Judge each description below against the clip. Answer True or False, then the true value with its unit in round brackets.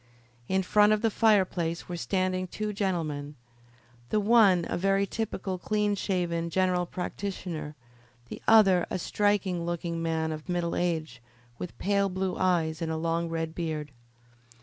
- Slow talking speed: False (150 wpm)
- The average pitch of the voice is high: False (180 Hz)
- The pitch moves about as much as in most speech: True (3.0 semitones)